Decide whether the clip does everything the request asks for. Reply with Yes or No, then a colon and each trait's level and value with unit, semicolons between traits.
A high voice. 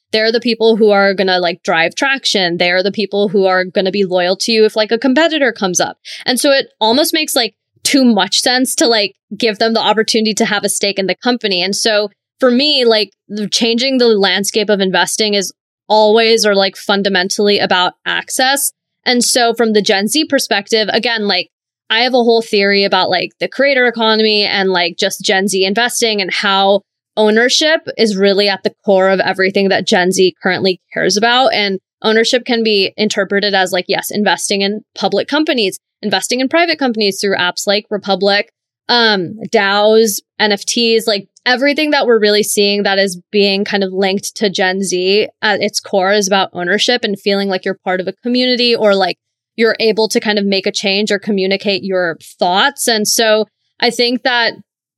Yes: high, 210 Hz